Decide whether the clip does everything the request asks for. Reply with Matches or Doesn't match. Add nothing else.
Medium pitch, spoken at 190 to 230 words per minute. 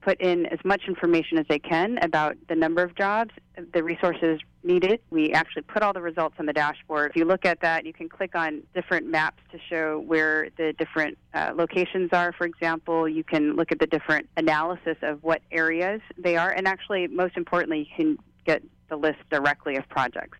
Matches